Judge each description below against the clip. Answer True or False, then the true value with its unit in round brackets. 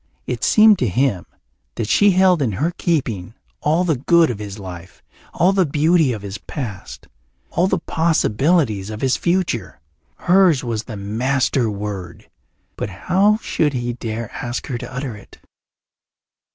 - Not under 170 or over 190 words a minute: False (155 wpm)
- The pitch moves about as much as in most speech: False (8.2 semitones)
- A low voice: True (130 Hz)